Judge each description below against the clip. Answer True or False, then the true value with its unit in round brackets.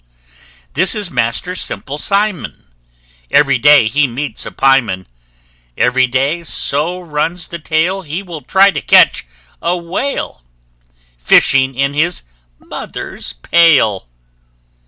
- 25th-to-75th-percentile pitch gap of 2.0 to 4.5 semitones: False (4.9 semitones)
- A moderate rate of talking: False (120 wpm)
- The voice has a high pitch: False (150 Hz)